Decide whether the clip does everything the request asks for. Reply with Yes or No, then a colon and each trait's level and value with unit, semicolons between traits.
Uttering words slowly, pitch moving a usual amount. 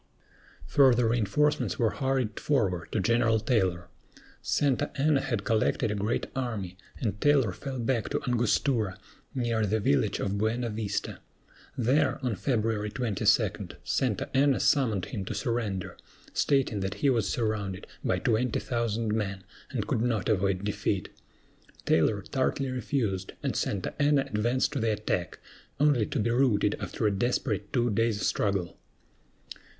No: average, 145 wpm; average, 3.8 semitones